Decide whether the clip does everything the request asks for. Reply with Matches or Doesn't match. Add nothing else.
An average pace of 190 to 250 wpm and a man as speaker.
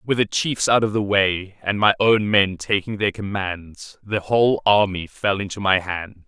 Matches